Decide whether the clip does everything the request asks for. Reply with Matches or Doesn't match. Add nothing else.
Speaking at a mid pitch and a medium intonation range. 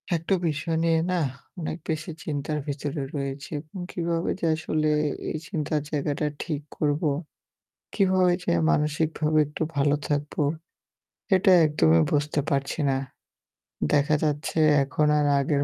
Doesn't match